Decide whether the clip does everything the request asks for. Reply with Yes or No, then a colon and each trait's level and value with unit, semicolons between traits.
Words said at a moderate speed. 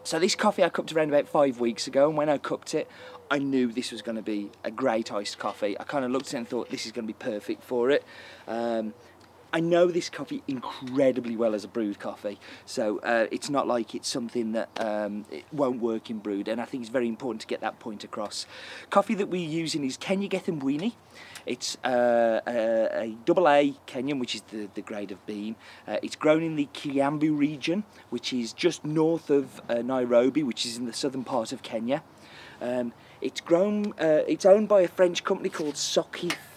No: fast, 220 wpm